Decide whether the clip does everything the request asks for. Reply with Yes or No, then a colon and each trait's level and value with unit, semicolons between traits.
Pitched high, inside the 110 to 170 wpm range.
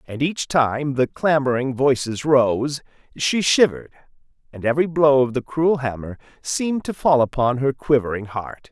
No: low, 135 Hz; average, 160 wpm